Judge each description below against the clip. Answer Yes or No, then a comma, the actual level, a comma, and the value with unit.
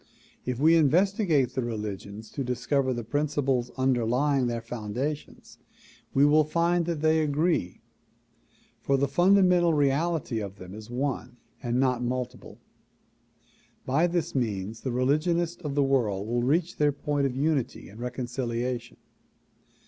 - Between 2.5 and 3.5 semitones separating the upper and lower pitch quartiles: No, average, 4.2 semitones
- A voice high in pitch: No, low, 135 Hz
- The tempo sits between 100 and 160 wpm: Yes, slow, 135 wpm